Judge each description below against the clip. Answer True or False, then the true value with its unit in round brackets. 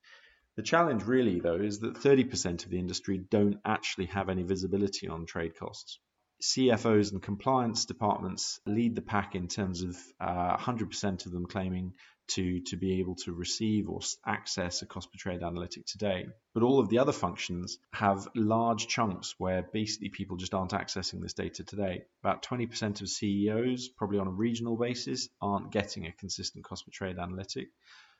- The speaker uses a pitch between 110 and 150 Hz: False (100 Hz)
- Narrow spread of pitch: False (3.8 semitones)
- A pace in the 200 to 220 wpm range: False (175 wpm)